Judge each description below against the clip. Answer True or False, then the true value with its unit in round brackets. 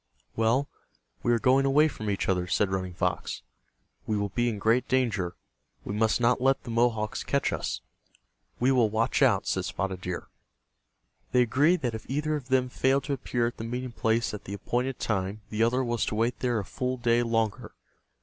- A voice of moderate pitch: False (120 Hz)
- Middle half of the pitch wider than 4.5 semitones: False (3.1 semitones)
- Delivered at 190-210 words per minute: True (200 wpm)